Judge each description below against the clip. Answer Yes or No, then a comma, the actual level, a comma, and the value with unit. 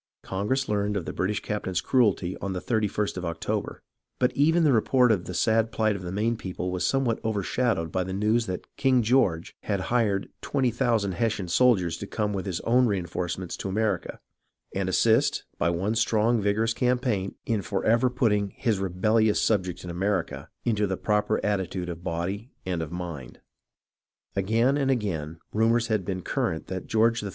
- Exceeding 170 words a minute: Yes, average, 180 wpm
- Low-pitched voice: Yes, low, 105 Hz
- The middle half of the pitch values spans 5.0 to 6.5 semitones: No, average, 3.8 semitones